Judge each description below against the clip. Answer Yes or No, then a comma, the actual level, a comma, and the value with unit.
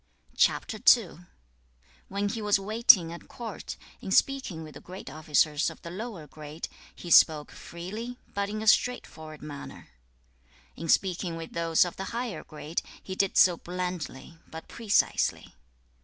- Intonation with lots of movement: No, average, 4.3 semitones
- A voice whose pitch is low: No, medium, 175 Hz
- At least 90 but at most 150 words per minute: Yes, average, 140 wpm